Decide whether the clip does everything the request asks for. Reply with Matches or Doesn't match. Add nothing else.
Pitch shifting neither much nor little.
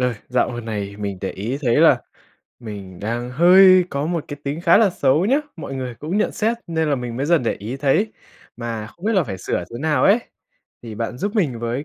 Doesn't match